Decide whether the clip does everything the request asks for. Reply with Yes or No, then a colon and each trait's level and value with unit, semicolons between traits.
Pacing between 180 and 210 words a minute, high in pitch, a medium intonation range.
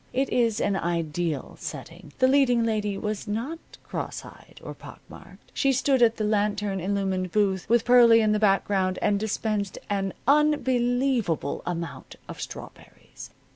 No: average, 150 wpm; high, 210 Hz; average, 3.9 semitones